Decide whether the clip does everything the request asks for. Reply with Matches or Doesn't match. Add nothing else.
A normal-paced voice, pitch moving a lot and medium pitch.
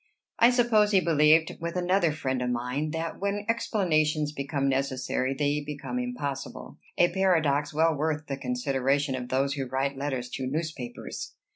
Doesn't match